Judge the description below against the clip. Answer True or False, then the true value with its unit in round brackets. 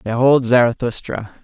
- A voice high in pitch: False (120 Hz)